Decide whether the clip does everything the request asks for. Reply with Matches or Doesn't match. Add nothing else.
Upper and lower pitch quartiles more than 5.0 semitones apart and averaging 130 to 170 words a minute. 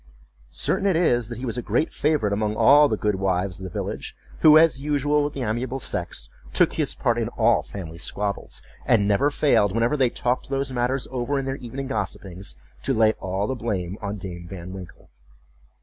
Doesn't match